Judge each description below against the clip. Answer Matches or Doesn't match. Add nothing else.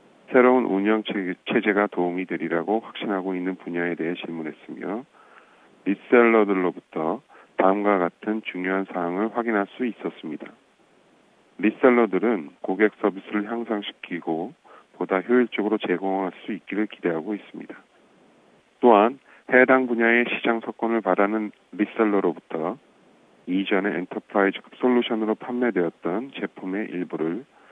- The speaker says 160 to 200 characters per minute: Doesn't match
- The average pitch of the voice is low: Matches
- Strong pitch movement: Doesn't match